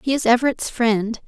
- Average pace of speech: Yes, average, 190 wpm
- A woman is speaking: Yes, female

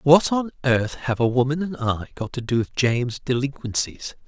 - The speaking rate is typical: Yes, average, 195 wpm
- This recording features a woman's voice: No, male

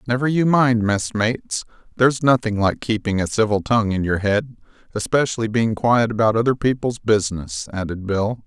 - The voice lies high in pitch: No, low, 110 Hz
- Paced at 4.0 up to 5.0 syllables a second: No, 5.4 syllables/s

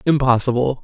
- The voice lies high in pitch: No, low, 130 Hz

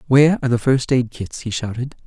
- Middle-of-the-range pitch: No, low, 125 Hz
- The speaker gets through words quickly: Yes, fast, 235 wpm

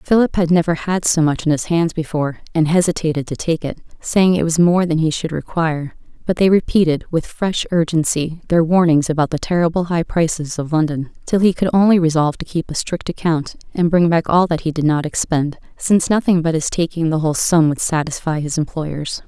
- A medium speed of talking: No, fast, 215 wpm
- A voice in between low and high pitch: Yes, medium, 165 Hz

